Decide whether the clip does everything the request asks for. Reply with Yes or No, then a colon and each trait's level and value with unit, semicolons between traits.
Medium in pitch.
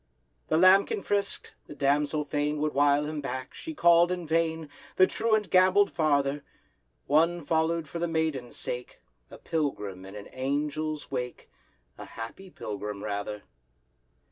Yes: medium, 150 Hz